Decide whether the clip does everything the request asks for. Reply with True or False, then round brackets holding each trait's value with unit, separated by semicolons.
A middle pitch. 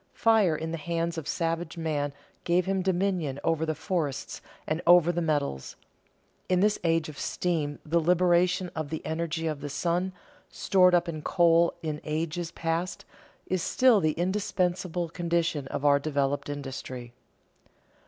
True (165 Hz)